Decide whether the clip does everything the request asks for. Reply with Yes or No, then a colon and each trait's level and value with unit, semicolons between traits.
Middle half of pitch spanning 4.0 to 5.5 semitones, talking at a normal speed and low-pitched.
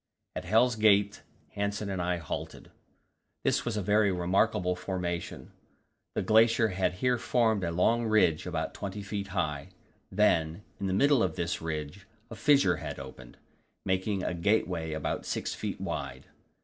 No: average, 3.6 semitones; average, 155 wpm; very low, 95 Hz